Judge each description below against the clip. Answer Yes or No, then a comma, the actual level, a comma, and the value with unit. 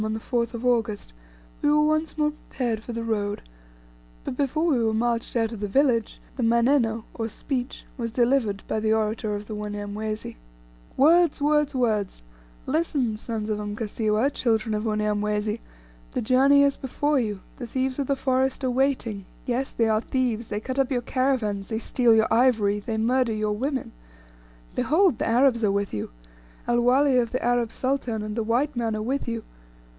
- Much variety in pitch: No, average, 3.5 semitones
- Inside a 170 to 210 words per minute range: Yes, average, 185 wpm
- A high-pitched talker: Yes, high, 235 Hz